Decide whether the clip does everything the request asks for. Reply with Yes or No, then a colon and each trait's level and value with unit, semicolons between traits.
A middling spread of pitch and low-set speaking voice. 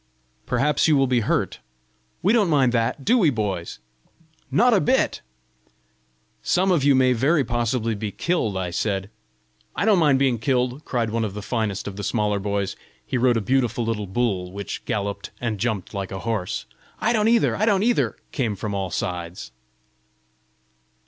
No: wide, 5.9 semitones; low, 120 Hz